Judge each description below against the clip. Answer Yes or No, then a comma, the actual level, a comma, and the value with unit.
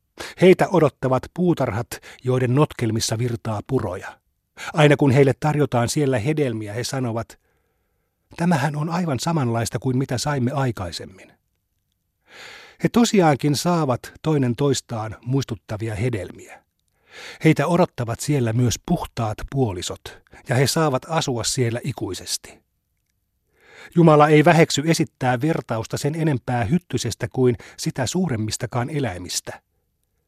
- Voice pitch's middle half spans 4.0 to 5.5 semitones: Yes, average, 4.9 semitones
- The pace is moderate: Yes, average, 105 wpm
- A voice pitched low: Yes, low, 130 Hz